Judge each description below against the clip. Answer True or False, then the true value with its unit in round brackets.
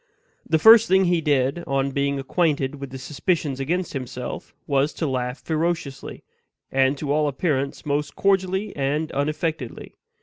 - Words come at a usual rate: True (145 wpm)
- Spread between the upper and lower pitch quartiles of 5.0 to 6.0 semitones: False (3.5 semitones)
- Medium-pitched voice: True (145 Hz)